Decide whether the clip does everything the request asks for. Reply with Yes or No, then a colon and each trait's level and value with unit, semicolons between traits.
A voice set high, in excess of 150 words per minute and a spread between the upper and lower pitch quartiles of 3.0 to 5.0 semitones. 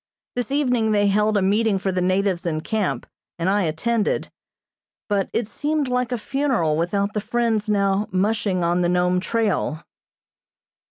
Yes: high, 205 Hz; average, 160 wpm; average, 3.8 semitones